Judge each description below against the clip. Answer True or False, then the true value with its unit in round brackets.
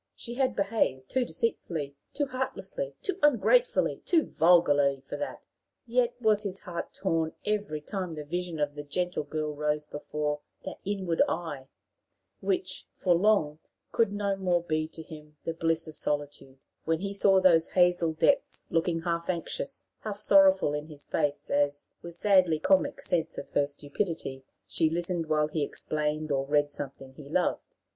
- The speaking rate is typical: True (165 wpm)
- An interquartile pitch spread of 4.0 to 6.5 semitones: True (4.8 semitones)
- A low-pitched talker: False (165 Hz)